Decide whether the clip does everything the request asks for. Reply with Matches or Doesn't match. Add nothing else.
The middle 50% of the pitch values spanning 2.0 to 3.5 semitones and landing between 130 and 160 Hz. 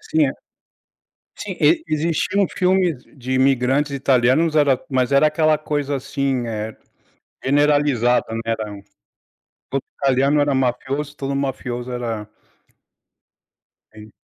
Matches